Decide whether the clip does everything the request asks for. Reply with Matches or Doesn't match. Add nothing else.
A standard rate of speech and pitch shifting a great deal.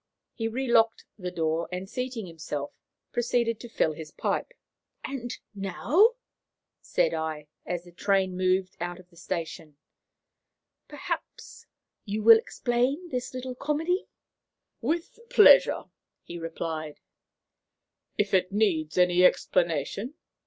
Doesn't match